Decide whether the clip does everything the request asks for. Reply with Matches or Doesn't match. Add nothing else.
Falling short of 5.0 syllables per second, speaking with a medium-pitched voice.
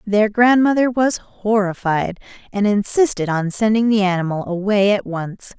Doesn't match